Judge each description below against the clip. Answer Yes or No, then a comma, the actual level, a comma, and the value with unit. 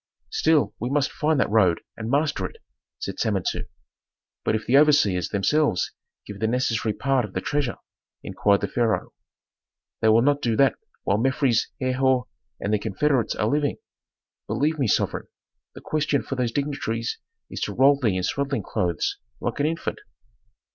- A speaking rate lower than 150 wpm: No, average, 165 wpm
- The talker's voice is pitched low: Yes, low, 125 Hz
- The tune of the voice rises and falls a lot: No, average, 4.8 semitones